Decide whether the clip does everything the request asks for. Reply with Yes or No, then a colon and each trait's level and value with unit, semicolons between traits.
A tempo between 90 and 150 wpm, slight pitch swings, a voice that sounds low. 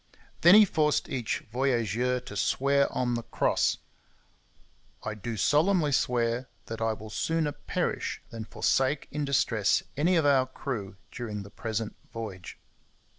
No: average, 140 wpm; average, 4.4 semitones; low, 125 Hz